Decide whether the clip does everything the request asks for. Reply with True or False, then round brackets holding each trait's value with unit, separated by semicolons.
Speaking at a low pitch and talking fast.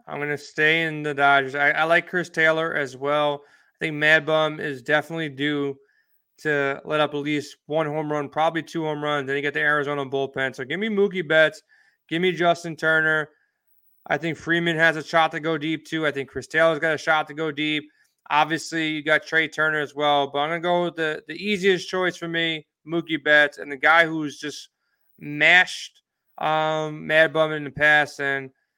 False (155 Hz; 215 wpm)